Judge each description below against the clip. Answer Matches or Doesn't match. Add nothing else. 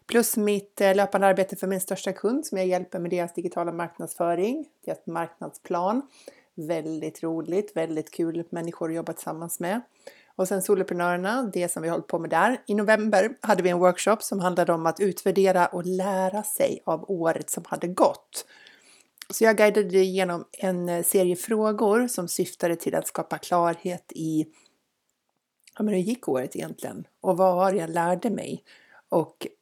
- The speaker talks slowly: Doesn't match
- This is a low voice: Doesn't match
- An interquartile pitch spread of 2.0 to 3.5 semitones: Matches